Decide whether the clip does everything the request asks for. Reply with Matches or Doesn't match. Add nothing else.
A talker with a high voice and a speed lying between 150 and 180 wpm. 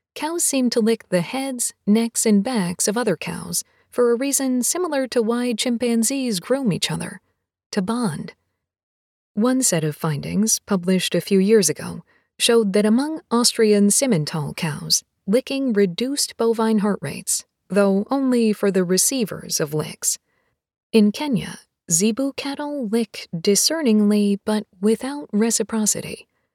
Doesn't match